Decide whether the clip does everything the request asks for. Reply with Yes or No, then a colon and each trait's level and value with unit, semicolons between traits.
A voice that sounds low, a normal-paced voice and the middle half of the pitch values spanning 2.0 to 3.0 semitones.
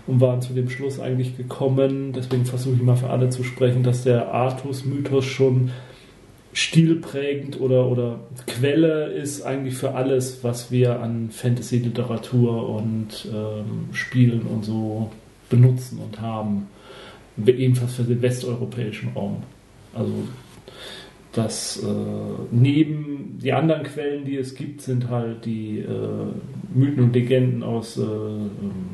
Yes: low, 125 Hz; average, 135 wpm; narrow, 2.5 semitones